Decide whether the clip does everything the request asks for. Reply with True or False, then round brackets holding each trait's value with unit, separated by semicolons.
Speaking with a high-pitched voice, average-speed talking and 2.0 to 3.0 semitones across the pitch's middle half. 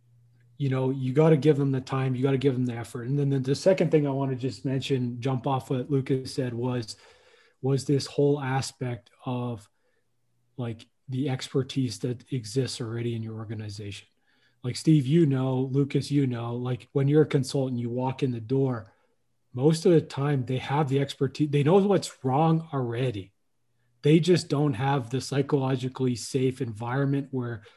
False (135 Hz; 185 wpm; 2.5 semitones)